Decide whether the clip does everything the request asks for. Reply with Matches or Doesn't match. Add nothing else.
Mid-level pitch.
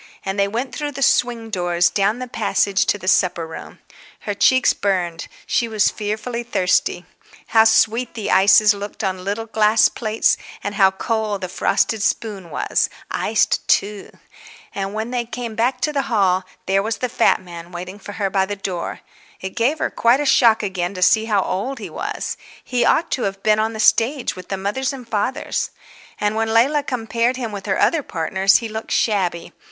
Doesn't match